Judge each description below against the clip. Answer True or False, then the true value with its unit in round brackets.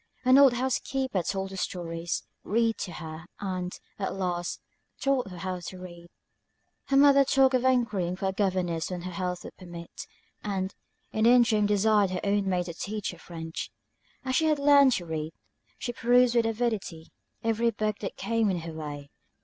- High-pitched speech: True (195 Hz)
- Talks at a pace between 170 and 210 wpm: True (180 wpm)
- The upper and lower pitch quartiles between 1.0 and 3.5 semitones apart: False (5.2 semitones)